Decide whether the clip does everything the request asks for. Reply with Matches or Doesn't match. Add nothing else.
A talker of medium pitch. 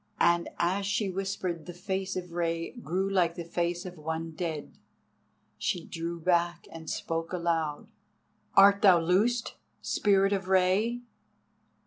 Matches